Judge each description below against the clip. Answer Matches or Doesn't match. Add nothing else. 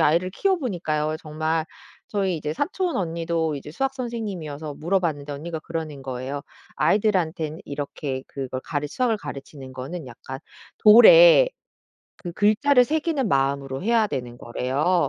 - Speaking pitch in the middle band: Matches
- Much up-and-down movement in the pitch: Matches